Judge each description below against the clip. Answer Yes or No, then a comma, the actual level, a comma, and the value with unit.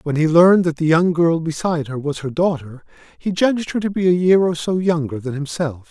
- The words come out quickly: Yes, fast, 245 wpm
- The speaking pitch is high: No, medium, 165 Hz